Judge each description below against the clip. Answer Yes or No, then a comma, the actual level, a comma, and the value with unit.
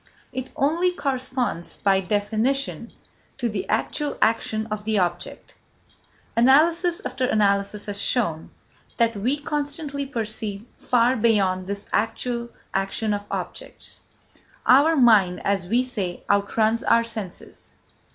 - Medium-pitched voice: No, high, 225 Hz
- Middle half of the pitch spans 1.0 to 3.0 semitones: No, average, 4.4 semitones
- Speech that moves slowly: Yes, slow, 120 wpm